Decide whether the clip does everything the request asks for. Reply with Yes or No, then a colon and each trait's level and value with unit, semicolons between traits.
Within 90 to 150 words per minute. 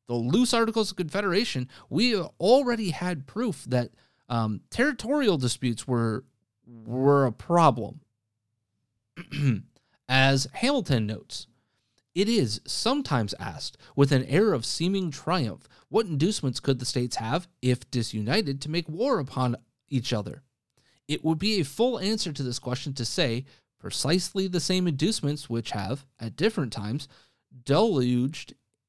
Yes: slow, 135 wpm